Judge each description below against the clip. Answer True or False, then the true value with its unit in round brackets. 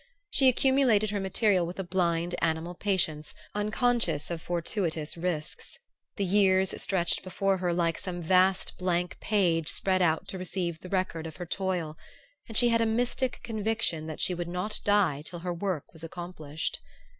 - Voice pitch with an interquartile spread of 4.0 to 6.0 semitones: False (3.2 semitones)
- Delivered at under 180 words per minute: True (170 wpm)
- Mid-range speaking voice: True (180 Hz)